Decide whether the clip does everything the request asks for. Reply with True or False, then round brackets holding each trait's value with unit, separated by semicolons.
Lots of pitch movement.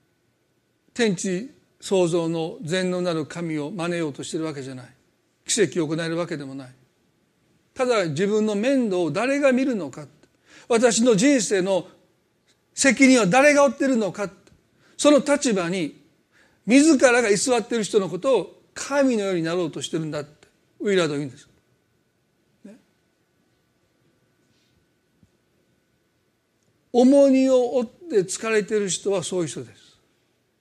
True (7.2 semitones)